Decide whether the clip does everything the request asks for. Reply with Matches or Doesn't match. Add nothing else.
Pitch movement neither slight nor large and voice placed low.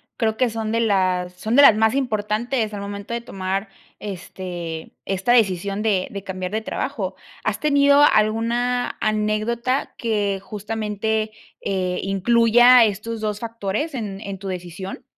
Doesn't match